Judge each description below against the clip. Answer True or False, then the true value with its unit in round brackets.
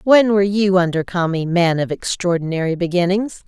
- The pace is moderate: True (155 wpm)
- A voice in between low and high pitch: True (180 Hz)